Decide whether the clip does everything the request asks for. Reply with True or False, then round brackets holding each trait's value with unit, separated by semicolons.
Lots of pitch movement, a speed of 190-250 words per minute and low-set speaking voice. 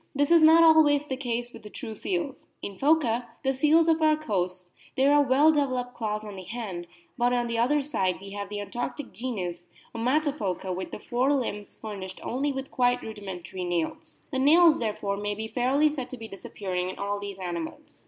False (6.1 semitones; 200 wpm; 240 Hz)